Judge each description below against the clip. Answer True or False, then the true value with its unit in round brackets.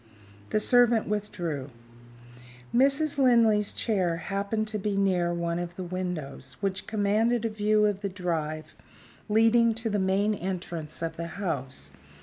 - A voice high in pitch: True (200 Hz)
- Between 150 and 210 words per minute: False (140 wpm)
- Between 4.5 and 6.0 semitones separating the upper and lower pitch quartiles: False (4.0 semitones)